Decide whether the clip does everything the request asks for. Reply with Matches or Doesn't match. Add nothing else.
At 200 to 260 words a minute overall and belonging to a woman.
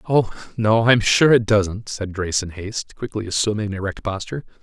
Doesn't match